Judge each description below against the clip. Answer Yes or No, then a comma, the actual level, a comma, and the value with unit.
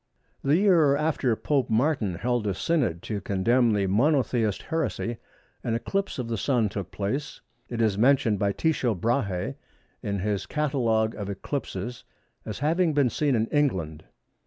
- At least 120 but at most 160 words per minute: Yes, average, 155 wpm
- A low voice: Yes, low, 120 Hz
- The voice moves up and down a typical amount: No, wide, 5.7 semitones